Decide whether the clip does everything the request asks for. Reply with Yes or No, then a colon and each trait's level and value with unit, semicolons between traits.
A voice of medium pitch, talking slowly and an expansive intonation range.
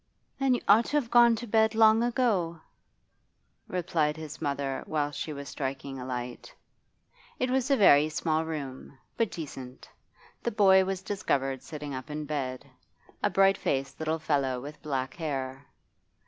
No: medium, 155 Hz; average, 160 wpm; wide, 6.9 semitones